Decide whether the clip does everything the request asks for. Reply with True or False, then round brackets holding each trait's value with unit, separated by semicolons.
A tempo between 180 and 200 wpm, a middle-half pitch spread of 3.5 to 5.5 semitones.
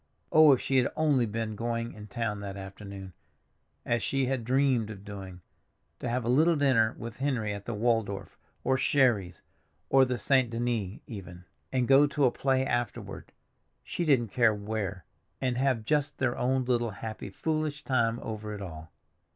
False (165 wpm; 4.1 semitones)